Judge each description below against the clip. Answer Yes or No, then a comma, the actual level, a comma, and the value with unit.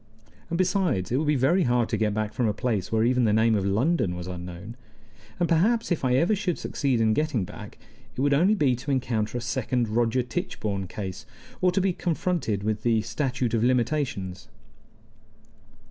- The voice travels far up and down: Yes, wide, 5.8 semitones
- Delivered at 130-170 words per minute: No, average, 190 wpm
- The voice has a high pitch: No, low, 120 Hz